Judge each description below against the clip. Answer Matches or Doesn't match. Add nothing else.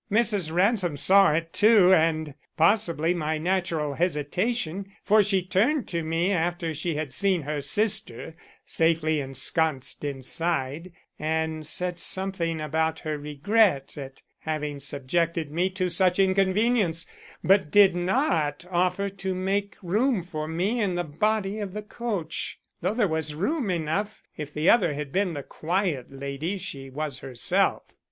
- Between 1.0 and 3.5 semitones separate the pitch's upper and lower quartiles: Doesn't match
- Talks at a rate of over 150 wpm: Doesn't match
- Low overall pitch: Doesn't match